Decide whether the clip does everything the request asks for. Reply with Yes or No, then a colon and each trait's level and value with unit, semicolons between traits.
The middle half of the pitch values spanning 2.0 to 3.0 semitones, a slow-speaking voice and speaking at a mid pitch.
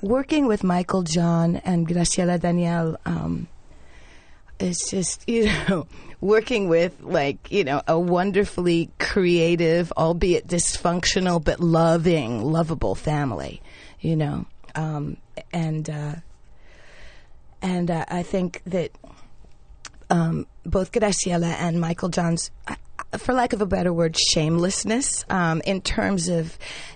Yes: narrow, 2.4 semitones; slow, 120 wpm; medium, 170 Hz